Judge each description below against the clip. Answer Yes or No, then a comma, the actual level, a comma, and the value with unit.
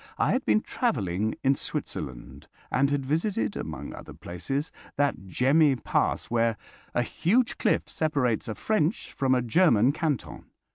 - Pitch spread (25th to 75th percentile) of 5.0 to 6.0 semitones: Yes, wide, 5.6 semitones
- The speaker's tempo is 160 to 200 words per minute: No, average, 145 wpm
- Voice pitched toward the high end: No, low, 135 Hz